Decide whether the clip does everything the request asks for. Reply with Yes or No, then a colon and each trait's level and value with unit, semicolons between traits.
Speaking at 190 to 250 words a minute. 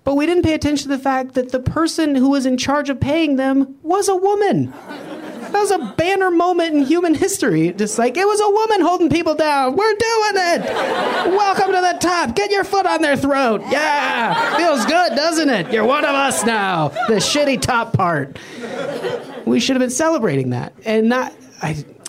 Yes: average, 200 wpm